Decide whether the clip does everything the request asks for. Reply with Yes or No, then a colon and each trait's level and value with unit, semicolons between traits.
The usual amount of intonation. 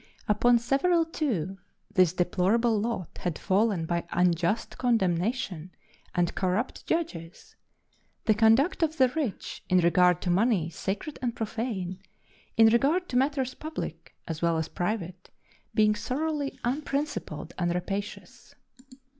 No: wide, 6.4 semitones